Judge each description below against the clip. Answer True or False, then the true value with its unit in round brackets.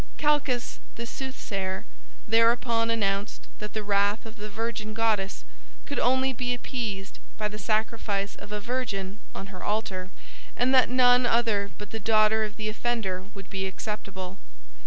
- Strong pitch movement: False (2.9 semitones)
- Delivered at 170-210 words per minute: False (155 wpm)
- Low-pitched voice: False (215 Hz)